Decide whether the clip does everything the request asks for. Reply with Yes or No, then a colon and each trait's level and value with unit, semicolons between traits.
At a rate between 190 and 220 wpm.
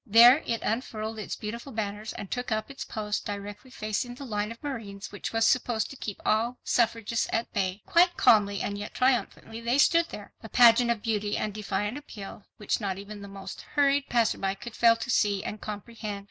Yes: average, 200 wpm